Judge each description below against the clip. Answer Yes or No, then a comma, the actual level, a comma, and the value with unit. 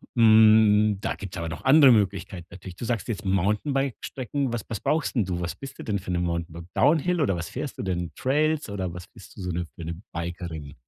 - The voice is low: Yes, low, 100 Hz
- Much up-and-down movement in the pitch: Yes, wide, 5.7 semitones